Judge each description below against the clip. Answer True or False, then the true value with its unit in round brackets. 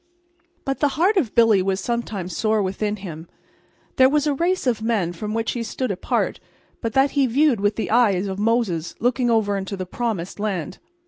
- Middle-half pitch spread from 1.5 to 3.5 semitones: False (4.3 semitones)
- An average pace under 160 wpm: False (195 wpm)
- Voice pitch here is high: True (220 Hz)